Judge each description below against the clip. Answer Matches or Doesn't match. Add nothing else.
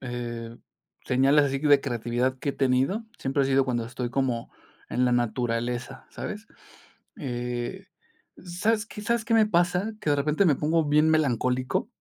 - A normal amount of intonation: Matches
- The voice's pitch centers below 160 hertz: Matches